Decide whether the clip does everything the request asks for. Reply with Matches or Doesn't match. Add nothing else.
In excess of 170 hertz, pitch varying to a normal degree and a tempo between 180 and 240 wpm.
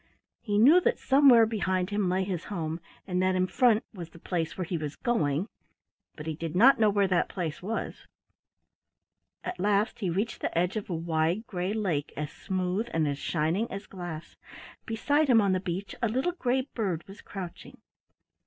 Matches